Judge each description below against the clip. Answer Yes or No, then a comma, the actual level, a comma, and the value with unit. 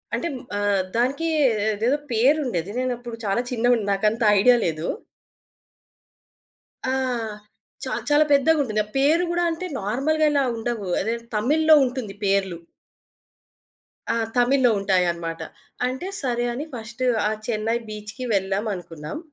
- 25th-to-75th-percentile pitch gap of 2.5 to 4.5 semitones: No, average, 5.0 semitones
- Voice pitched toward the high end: Yes, high, 235 Hz